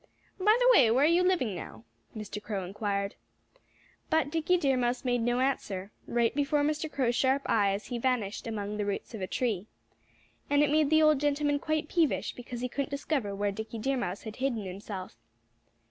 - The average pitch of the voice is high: Yes, high, 245 Hz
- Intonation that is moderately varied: No, wide, 5.8 semitones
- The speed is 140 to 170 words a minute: No, average, 190 wpm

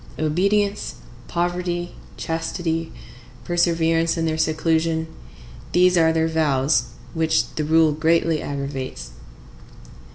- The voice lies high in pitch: No, medium, 160 Hz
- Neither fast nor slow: No, slow, 90 wpm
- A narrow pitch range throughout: Yes, narrow, 1.6 semitones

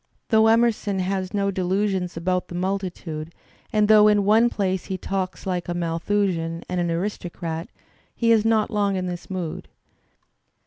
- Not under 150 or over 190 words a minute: Yes, average, 165 wpm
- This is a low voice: No, high, 190 Hz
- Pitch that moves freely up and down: No, average, 2.9 semitones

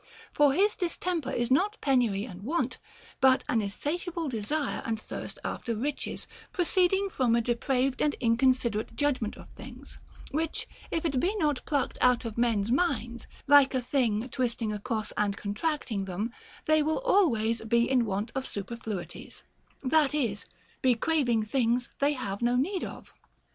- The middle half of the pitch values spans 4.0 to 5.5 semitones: Yes, average, 4.7 semitones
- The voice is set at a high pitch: Yes, very high, 250 Hz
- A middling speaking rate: Yes, average, 155 wpm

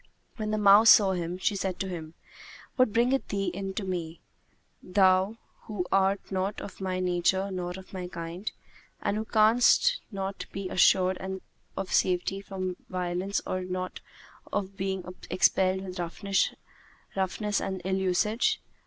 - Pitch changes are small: Yes, narrow, 1.6 semitones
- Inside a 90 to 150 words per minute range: Yes, average, 145 wpm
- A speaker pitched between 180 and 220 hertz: Yes, high, 190 Hz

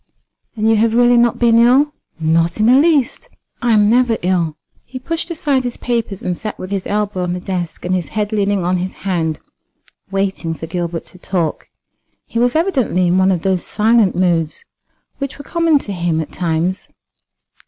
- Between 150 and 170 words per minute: No, average, 190 wpm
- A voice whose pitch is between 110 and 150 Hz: No, high, 200 Hz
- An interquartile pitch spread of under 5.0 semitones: No, average, 5.3 semitones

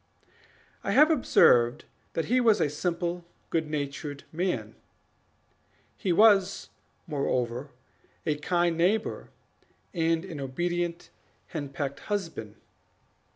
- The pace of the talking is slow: Yes, slow, 100 wpm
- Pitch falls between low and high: Yes, medium, 165 Hz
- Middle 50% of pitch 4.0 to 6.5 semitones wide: Yes, average, 4.6 semitones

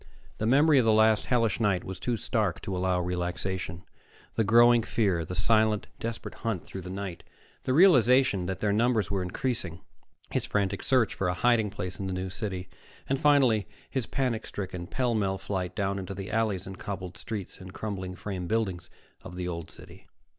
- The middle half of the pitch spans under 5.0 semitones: Yes, average, 3.7 semitones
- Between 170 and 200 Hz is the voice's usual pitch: No, low, 100 Hz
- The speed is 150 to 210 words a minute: Yes, average, 190 wpm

